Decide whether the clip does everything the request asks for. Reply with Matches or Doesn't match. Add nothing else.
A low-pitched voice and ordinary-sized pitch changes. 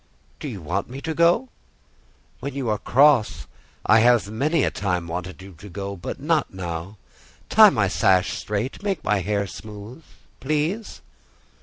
Doesn't match